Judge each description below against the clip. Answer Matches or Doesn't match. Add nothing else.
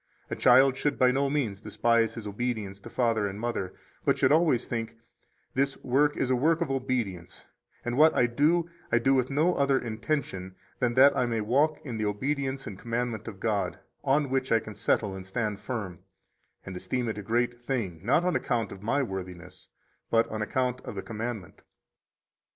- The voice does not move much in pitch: Doesn't match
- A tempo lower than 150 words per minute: Doesn't match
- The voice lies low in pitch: Matches